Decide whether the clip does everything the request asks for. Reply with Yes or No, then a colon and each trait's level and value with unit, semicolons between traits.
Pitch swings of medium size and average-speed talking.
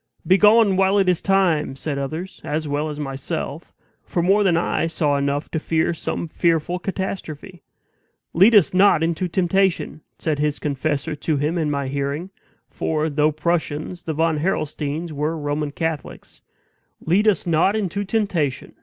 Yes: average, 3.7 semitones; average, 155 wpm